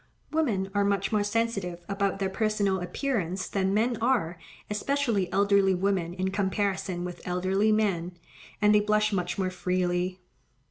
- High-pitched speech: Yes, high, 195 Hz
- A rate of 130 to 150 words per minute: Yes, average, 145 wpm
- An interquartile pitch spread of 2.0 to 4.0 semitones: Yes, narrow, 2.5 semitones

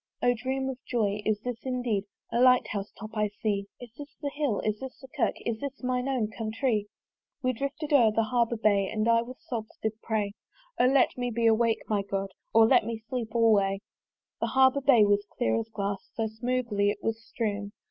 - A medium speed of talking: No, fast, 210 wpm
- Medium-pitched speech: No, high, 225 Hz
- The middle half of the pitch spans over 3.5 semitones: No, average, 3.1 semitones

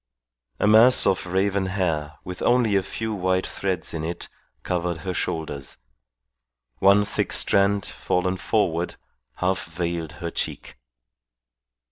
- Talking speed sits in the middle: No, slow, 125 wpm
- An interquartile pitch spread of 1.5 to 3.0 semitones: Yes, average, 2.7 semitones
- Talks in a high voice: No, very low, 95 Hz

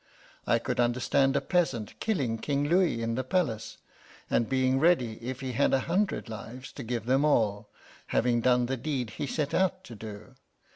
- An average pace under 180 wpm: No, average, 185 wpm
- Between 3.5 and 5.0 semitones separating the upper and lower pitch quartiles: Yes, average, 4.0 semitones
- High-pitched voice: No, low, 130 Hz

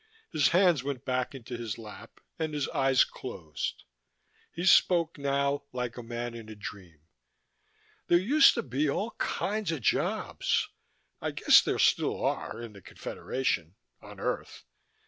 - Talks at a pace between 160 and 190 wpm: No, average, 150 wpm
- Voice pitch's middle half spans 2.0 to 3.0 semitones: No, average, 5.3 semitones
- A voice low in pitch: Yes, low, 130 Hz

